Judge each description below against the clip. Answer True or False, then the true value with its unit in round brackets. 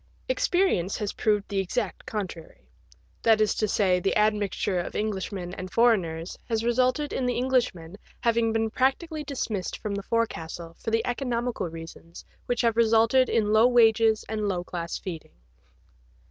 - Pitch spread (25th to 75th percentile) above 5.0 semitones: False (4.2 semitones)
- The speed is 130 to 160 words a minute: True (155 wpm)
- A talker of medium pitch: False (215 Hz)